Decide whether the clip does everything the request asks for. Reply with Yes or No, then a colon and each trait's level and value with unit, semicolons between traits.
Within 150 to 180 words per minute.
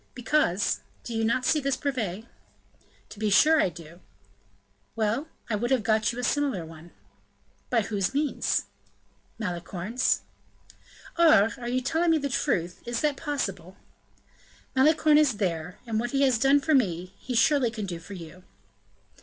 Yes: average, 155 wpm